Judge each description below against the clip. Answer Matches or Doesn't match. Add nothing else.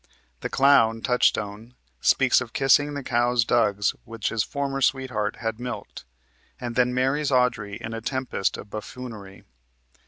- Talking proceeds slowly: Doesn't match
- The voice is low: Matches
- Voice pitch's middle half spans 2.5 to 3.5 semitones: Matches